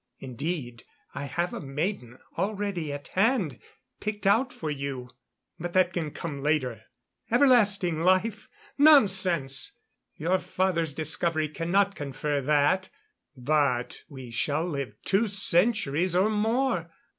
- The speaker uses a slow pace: Yes, slow, 120 wpm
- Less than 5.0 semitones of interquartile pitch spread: No, wide, 5.6 semitones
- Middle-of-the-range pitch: Yes, medium, 170 Hz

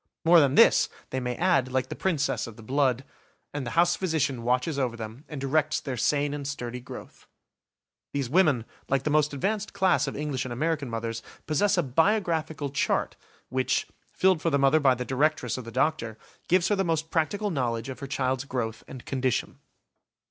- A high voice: No, medium, 140 Hz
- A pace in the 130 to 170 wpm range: No, average, 190 wpm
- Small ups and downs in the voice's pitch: No, average, 4.0 semitones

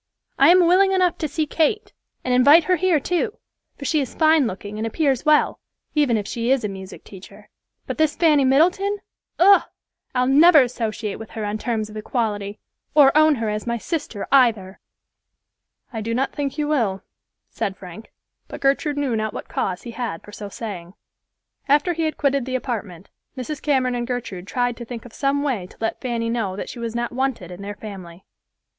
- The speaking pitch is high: Yes, very high, 250 Hz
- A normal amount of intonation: No, wide, 5.7 semitones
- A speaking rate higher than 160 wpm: Yes, average, 195 wpm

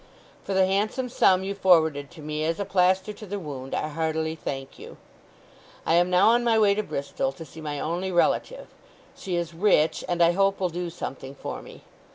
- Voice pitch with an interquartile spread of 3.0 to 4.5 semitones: Yes, average, 3.8 semitones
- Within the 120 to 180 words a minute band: No, fast, 205 wpm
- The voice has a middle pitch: Yes, medium, 175 Hz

